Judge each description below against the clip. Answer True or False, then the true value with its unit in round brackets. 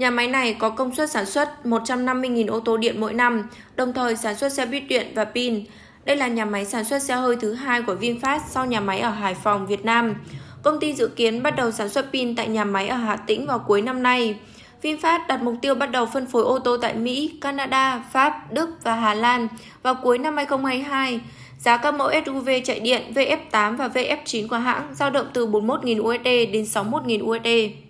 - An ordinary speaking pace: True (220 wpm)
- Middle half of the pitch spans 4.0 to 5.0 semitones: False (3.1 semitones)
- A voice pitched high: True (245 Hz)